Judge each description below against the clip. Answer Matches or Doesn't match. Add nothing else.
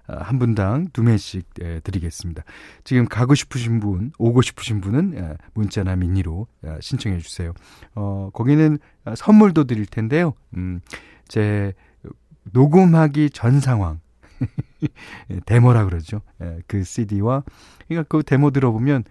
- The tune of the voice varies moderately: Doesn't match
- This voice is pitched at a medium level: Doesn't match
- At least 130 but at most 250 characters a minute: Matches